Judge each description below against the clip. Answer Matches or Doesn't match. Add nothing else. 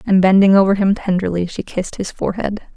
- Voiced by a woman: Matches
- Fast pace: Doesn't match